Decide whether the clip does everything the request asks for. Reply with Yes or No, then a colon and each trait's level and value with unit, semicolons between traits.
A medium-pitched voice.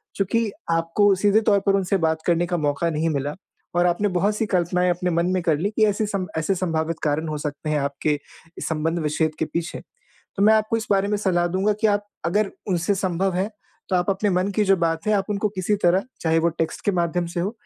Yes: medium, 180 Hz